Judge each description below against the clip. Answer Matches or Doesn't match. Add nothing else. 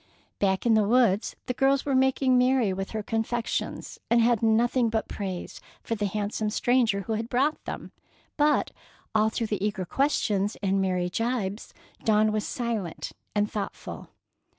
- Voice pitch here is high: Matches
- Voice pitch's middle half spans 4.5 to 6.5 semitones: Doesn't match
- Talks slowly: Doesn't match